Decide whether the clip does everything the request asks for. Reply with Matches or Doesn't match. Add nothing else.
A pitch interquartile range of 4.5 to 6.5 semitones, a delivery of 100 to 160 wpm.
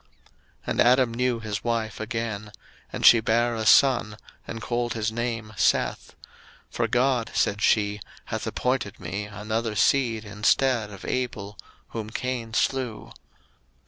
Doesn't match